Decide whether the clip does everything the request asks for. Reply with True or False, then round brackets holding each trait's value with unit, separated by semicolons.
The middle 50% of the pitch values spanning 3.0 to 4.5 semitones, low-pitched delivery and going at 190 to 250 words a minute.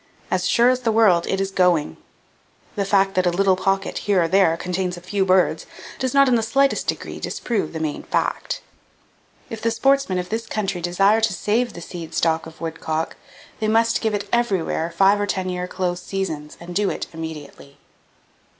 False (3.8 semitones; 190 Hz; 195 wpm)